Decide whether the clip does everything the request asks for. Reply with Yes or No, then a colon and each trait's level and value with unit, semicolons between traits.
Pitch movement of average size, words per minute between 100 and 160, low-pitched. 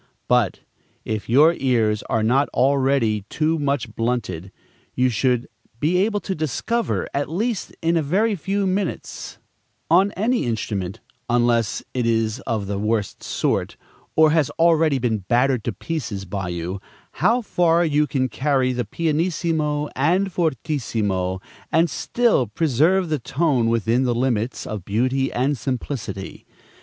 No: wide, 6.3 semitones; average, 140 wpm; low, 130 Hz